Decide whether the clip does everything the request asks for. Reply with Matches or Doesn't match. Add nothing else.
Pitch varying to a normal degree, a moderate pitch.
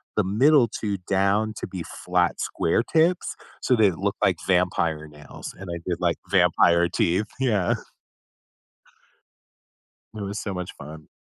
Doesn't match